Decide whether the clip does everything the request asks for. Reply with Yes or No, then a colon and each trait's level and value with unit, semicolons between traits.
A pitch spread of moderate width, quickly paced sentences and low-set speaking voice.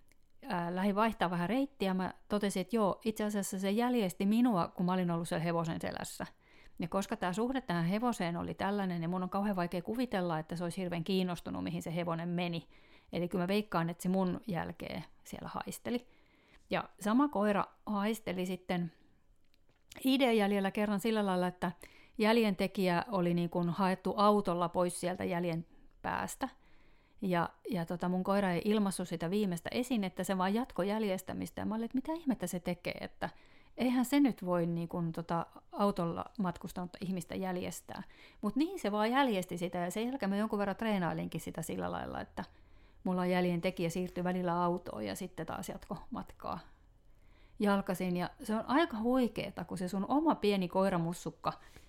No: average, 3.3 semitones; fast, 175 wpm; medium, 185 Hz